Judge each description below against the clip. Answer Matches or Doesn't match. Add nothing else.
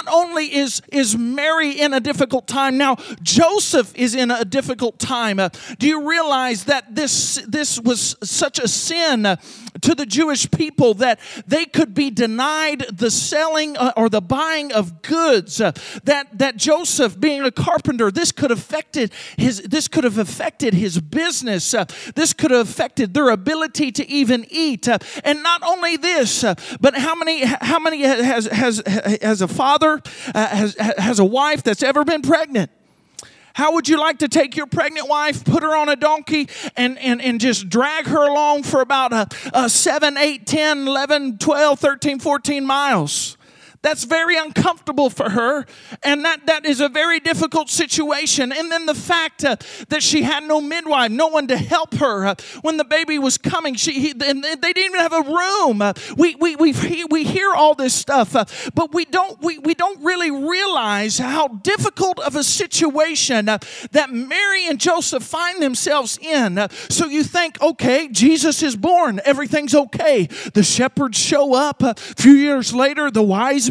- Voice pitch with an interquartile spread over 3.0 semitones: Matches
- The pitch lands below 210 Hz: Doesn't match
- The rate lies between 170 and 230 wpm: Matches